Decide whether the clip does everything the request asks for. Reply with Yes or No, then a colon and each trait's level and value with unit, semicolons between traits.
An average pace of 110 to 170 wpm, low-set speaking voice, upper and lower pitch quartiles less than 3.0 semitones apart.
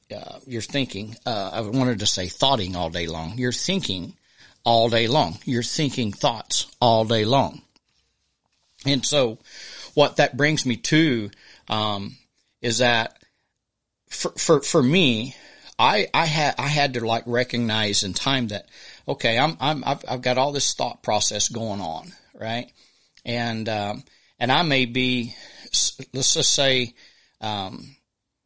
No: average, 150 wpm; low, 120 Hz; average, 3.7 semitones